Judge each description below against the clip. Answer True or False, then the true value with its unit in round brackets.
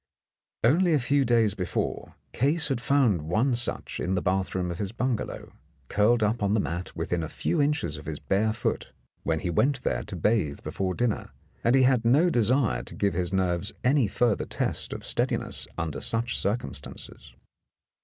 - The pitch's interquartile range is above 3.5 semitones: True (5.6 semitones)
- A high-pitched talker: False (110 Hz)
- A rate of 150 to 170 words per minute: False (180 wpm)